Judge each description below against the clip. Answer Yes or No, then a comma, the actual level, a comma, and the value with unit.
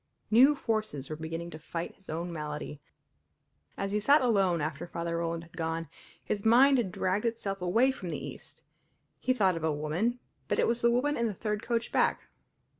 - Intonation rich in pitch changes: Yes, wide, 5.9 semitones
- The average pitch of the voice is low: No, high, 190 Hz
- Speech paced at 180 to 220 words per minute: Yes, average, 195 wpm